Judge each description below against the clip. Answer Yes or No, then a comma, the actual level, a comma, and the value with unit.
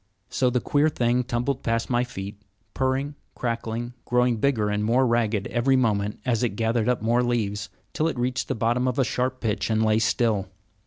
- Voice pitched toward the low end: Yes, low, 120 Hz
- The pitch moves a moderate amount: No, narrow, 2.2 semitones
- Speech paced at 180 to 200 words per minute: Yes, average, 195 wpm